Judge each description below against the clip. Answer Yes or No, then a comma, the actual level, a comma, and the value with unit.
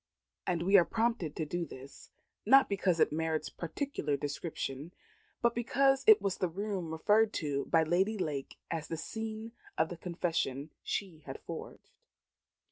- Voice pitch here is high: No, medium, 175 Hz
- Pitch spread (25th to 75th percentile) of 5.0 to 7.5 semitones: Yes, wide, 5.4 semitones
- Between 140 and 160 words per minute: Yes, average, 155 wpm